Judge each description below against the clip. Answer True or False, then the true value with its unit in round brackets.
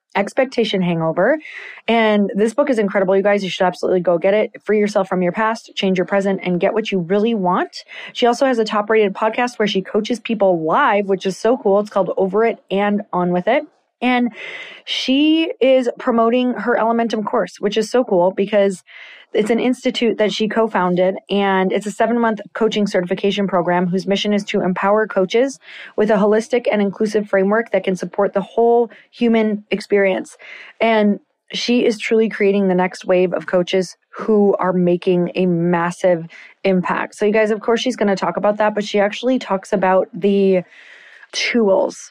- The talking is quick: False (190 wpm)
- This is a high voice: True (205 Hz)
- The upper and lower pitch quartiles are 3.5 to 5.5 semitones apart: False (3.0 semitones)